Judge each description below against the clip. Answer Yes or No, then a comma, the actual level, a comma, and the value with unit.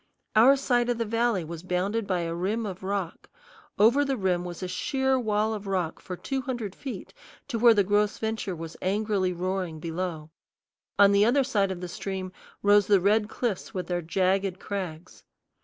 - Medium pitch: No, high, 200 Hz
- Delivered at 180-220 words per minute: Yes, average, 190 wpm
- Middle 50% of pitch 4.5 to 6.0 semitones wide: No, average, 3.5 semitones